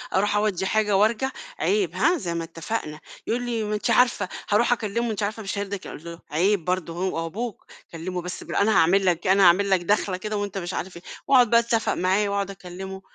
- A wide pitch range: No, average, 3.2 semitones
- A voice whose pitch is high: Yes, high, 200 Hz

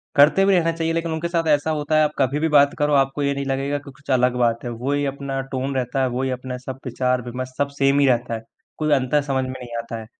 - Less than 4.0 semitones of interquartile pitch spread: Yes, narrow, 2.6 semitones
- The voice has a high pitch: No, low, 135 Hz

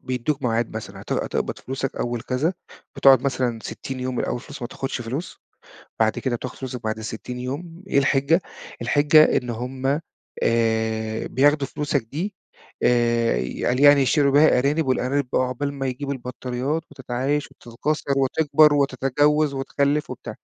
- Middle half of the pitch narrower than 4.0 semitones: Yes, average, 2.9 semitones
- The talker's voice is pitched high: No, low, 135 Hz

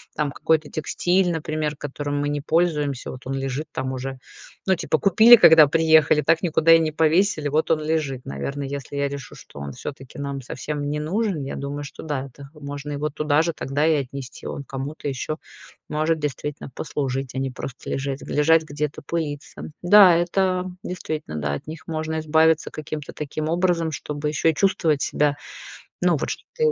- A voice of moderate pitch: Yes, medium, 150 Hz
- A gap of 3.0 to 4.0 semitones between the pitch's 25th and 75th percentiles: No, narrow, 2.4 semitones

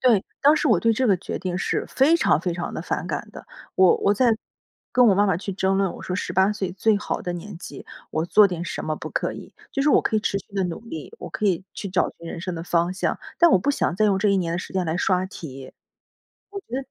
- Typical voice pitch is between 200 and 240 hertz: No, high, 190 Hz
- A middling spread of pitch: Yes, average, 3.5 semitones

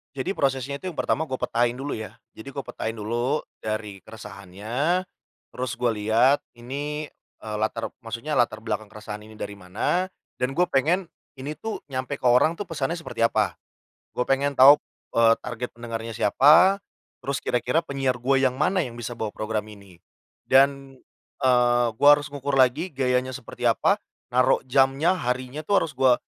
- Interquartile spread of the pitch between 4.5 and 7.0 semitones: No, average, 3.8 semitones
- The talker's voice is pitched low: Yes, low, 125 Hz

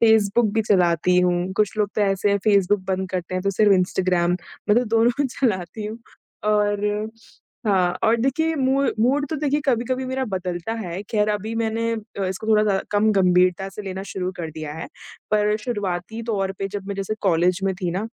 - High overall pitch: Yes, high, 205 Hz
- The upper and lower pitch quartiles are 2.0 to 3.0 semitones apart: No, average, 3.4 semitones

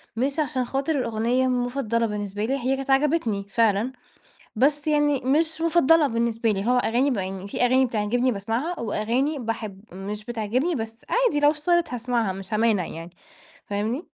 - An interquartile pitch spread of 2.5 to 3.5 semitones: No, average, 4.6 semitones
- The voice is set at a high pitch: Yes, high, 245 Hz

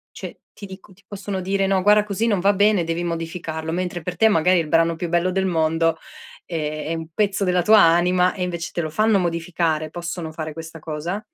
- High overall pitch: No, medium, 175 Hz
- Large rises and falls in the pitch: No, average, 2.7 semitones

